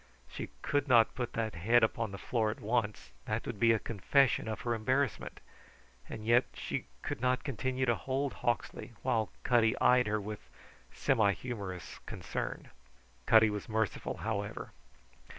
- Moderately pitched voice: No, low, 115 Hz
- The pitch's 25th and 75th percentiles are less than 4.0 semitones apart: Yes, average, 2.9 semitones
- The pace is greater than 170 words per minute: No, average, 155 wpm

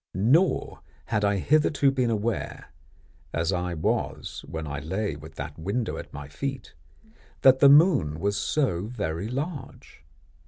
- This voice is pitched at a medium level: No, low, 100 Hz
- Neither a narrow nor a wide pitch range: No, wide, 8.9 semitones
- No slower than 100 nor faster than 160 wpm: Yes, average, 145 wpm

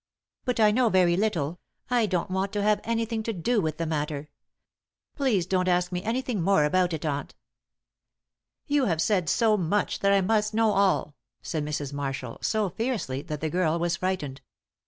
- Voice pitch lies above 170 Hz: Yes, medium, 185 Hz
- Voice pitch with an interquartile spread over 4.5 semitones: Yes, average, 5.2 semitones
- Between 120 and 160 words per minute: No, average, 180 wpm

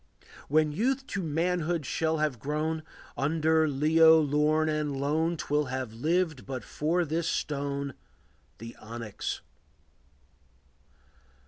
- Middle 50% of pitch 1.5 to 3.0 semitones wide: Yes, narrow, 2.4 semitones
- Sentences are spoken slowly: Yes, slow, 110 wpm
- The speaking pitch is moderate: Yes, medium, 155 Hz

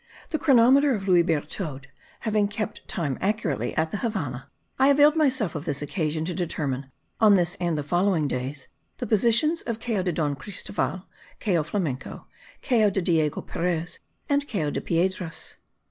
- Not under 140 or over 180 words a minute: Yes, average, 160 wpm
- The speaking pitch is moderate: Yes, medium, 180 Hz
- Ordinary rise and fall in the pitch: No, wide, 6.1 semitones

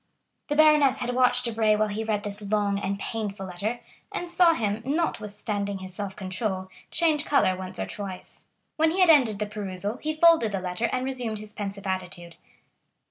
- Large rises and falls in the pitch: No, average, 4.5 semitones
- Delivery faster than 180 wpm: Yes, average, 190 wpm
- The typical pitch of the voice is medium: No, high, 210 Hz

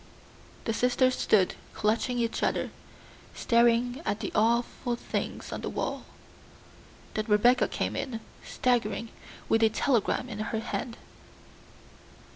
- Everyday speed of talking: No, slow, 120 wpm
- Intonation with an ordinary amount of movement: No, narrow, 2.0 semitones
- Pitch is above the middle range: Yes, high, 230 Hz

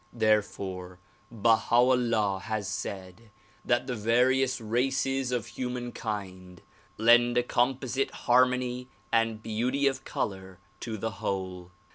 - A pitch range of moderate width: Yes, average, 3.7 semitones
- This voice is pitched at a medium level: No, low, 115 Hz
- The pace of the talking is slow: Yes, slow, 120 wpm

